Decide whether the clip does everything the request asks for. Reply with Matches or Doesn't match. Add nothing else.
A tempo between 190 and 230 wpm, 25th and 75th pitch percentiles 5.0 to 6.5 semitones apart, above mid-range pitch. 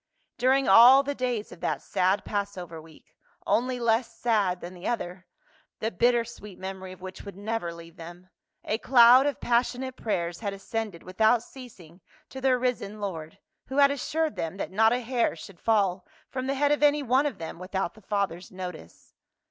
Matches